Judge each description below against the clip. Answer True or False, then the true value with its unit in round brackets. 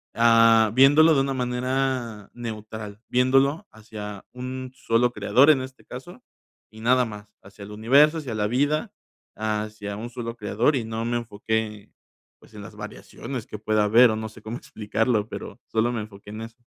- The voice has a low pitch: True (115 Hz)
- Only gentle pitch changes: False (3.0 semitones)